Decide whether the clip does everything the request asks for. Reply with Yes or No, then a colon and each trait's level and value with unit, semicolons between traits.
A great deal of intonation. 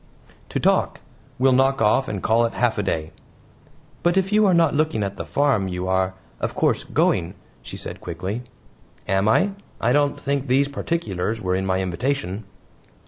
Yes: wide, 6.9 semitones